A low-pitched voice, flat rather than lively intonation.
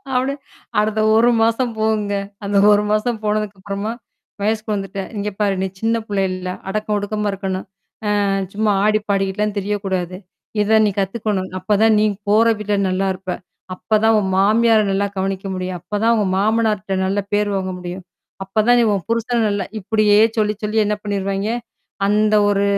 No: high, 210 Hz; narrow, 1.8 semitones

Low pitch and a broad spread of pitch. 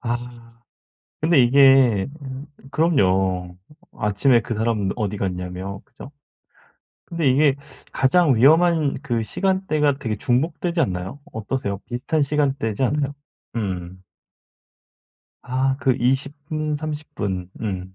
Yes: low, 125 Hz; wide, 6.0 semitones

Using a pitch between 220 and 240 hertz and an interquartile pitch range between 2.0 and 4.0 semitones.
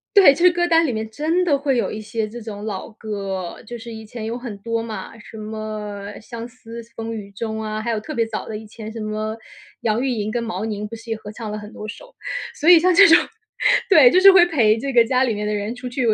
Yes: high, 225 Hz; average, 2.9 semitones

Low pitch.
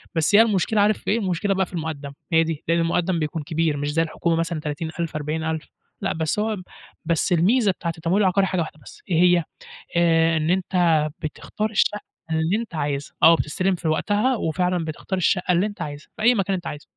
No: medium, 170 Hz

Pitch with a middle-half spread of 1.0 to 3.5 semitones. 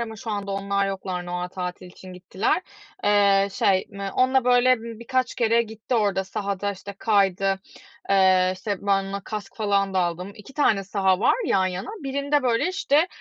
Yes: average, 3.2 semitones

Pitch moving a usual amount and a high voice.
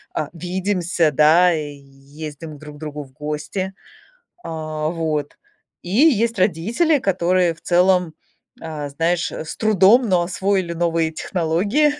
No: average, 3.7 semitones; medium, 170 Hz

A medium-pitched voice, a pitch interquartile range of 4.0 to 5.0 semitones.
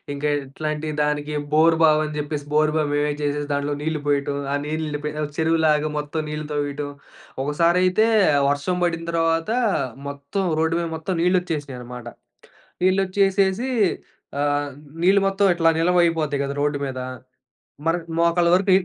No: medium, 155 Hz; narrow, 2.6 semitones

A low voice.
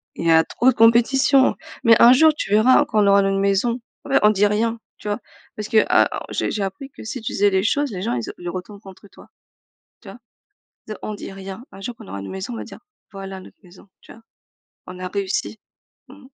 No: high, 205 Hz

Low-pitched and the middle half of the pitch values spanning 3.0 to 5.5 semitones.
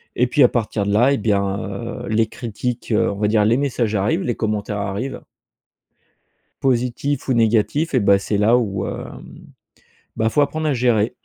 Yes: low, 115 Hz; average, 3.3 semitones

